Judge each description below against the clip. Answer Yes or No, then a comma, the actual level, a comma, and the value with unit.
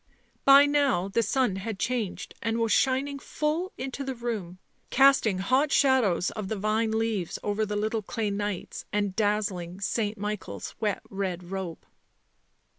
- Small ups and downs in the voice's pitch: No, average, 4.6 semitones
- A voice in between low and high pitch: No, high, 215 Hz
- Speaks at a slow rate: No, average, 150 wpm